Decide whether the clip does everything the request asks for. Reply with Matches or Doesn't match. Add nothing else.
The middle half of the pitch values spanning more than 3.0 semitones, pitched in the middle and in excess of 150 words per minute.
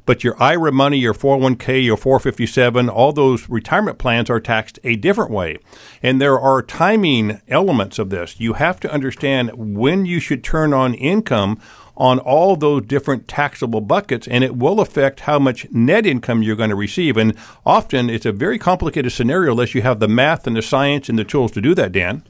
Doesn't match